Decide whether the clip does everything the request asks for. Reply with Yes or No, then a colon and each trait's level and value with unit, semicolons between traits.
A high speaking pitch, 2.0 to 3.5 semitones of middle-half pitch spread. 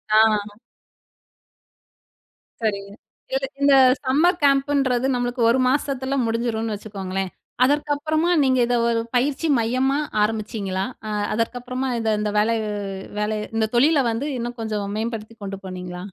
No: high, 235 Hz; average, 3.9 semitones